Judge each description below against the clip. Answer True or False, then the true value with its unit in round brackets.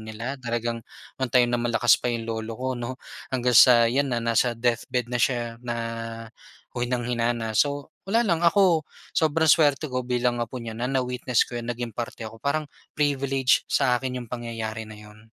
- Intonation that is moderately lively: False (2.1 semitones)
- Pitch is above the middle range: False (120 Hz)